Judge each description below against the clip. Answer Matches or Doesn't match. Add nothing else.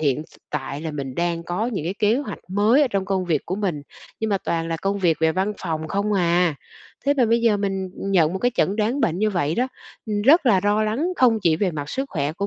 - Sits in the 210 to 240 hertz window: Doesn't match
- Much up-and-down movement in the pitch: Doesn't match